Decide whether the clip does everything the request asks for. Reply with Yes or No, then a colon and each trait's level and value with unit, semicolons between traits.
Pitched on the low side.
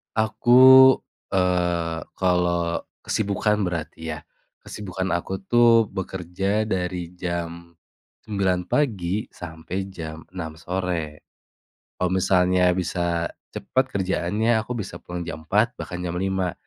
Yes: very low, 90 Hz